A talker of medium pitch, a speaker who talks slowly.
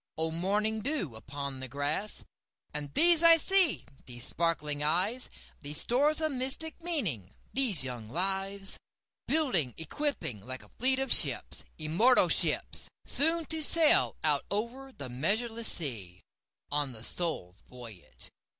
Yes: medium, 180 Hz; slow, 110 wpm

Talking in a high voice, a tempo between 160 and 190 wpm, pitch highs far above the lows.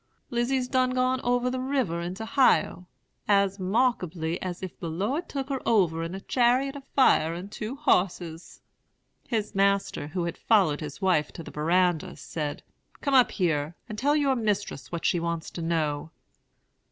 Yes: high, 195 Hz; average, 170 wpm; wide, 7.0 semitones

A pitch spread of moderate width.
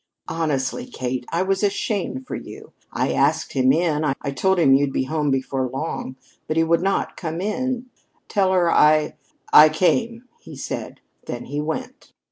No: wide, 5.8 semitones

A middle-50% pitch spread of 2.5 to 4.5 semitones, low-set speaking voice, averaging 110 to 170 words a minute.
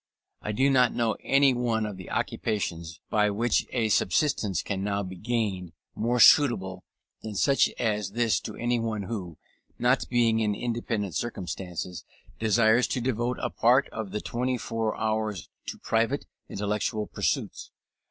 Yes: average, 2.9 semitones; low, 110 Hz; average, 150 wpm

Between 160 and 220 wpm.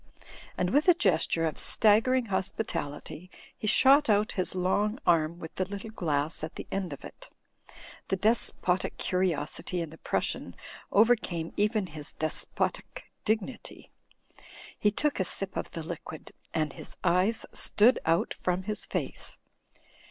No: average, 145 wpm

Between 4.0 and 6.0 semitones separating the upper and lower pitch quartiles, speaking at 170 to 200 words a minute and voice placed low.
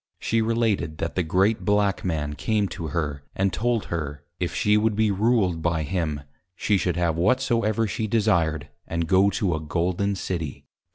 Yes: average, 4.5 semitones; average, 175 wpm; very low, 95 Hz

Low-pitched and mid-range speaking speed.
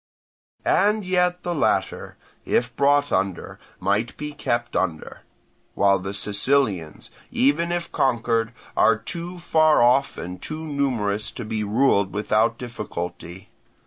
No: low, 120 Hz; slow, 125 wpm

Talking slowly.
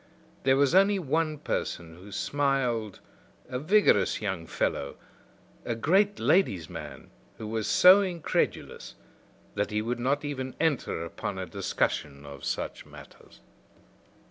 Yes: slow, 130 wpm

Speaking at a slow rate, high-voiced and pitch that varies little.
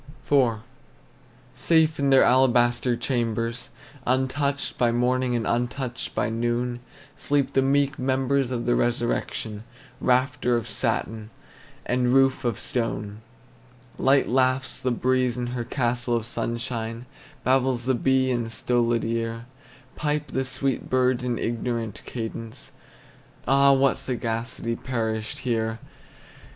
No: slow, 125 wpm; low, 125 Hz; narrow, 2.1 semitones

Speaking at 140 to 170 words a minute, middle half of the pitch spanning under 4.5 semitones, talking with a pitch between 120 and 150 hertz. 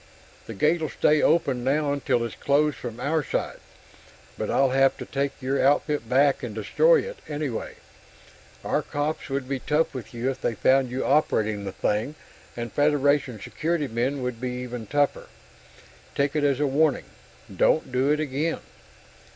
Yes: average, 165 wpm; average, 3.0 semitones; medium, 140 Hz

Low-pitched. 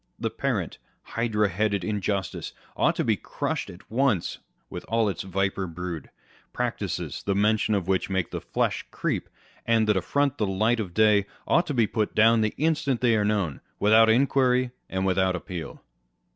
Yes: low, 105 Hz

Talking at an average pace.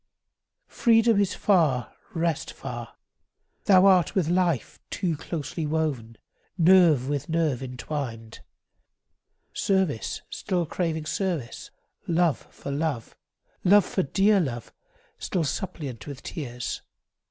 No: slow, 105 wpm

